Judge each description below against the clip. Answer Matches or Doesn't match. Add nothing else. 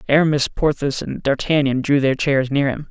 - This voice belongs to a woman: Doesn't match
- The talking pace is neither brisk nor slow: Matches